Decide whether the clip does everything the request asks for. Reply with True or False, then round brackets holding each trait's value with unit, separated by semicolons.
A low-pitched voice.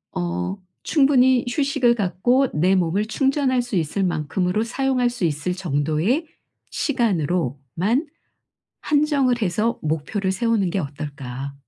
False (195 Hz)